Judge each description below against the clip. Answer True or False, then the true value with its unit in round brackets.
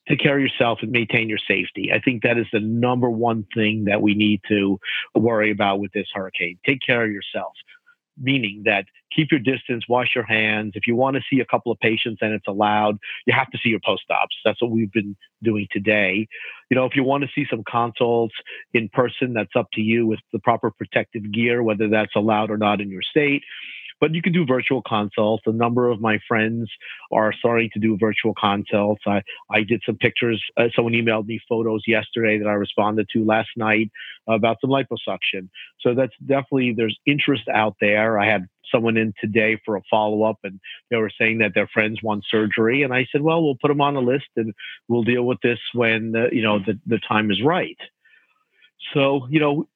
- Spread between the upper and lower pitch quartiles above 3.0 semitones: False (2.6 semitones)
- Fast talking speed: True (215 wpm)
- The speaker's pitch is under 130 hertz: True (115 Hz)